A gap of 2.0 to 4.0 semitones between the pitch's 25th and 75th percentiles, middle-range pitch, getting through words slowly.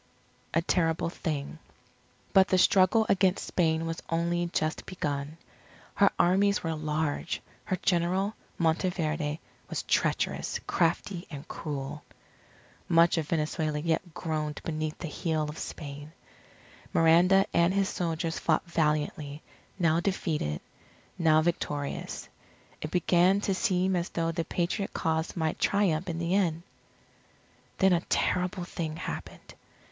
Yes: narrow, 2.6 semitones; medium, 165 Hz; slow, 125 wpm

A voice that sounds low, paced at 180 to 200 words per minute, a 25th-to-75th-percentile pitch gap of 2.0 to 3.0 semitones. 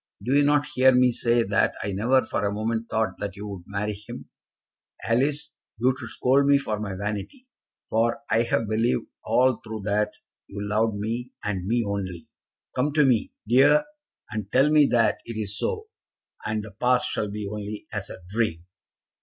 No: low, 110 Hz; average, 185 wpm; average, 3.6 semitones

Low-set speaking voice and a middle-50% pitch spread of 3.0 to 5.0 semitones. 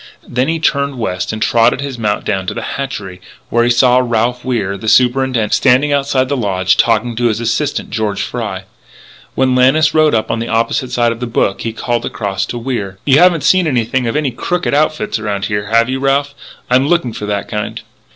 Yes: low, 120 Hz; average, 3.8 semitones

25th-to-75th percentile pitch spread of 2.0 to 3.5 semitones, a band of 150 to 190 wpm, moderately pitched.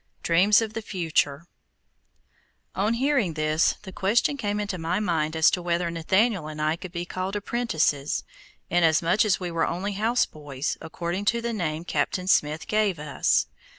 No: average, 4.4 semitones; average, 160 wpm; medium, 180 Hz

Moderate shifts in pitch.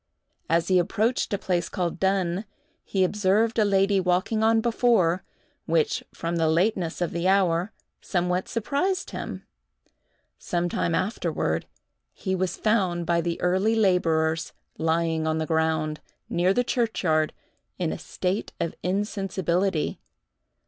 Yes: average, 3.2 semitones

